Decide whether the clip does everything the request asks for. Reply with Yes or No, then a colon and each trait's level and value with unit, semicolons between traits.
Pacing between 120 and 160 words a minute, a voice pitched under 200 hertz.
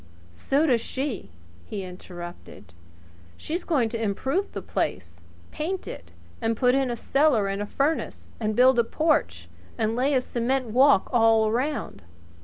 No: average, 155 wpm; high, 240 Hz